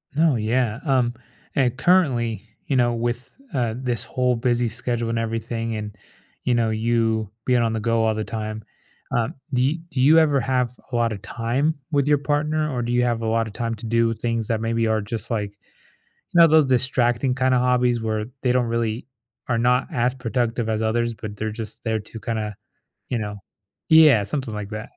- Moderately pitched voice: No, low, 120 Hz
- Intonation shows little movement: Yes, narrow, 2.1 semitones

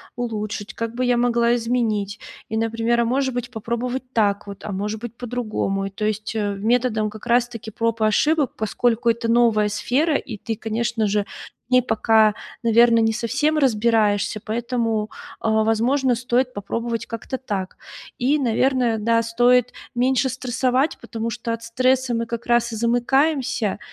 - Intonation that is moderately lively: No, narrow, 2.2 semitones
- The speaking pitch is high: Yes, high, 230 Hz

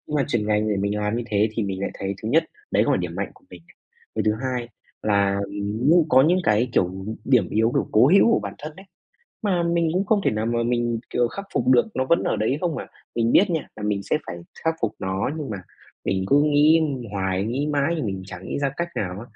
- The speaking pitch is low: Yes, low, 120 Hz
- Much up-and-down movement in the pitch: Yes, wide, 6.5 semitones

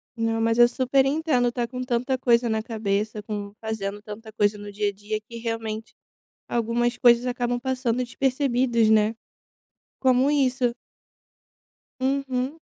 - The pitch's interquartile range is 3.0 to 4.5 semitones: No, narrow, 2.6 semitones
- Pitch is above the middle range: Yes, high, 235 Hz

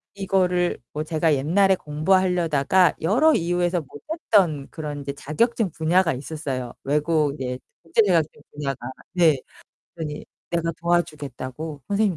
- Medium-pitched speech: Yes, medium, 160 Hz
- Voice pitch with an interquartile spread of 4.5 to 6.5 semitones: No, average, 3.6 semitones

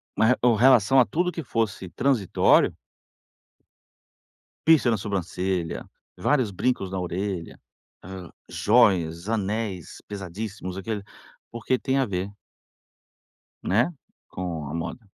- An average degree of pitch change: Yes, average, 4.5 semitones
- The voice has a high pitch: No, low, 100 Hz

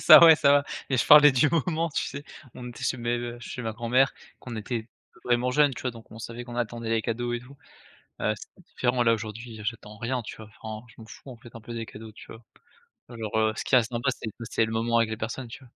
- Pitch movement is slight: Yes, narrow, 2.2 semitones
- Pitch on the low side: Yes, low, 120 Hz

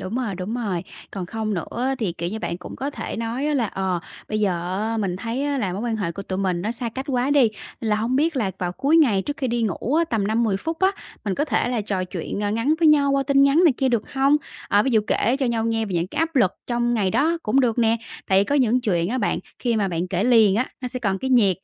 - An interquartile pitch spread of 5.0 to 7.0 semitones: Yes, average, 5.3 semitones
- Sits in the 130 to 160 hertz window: No, high, 225 Hz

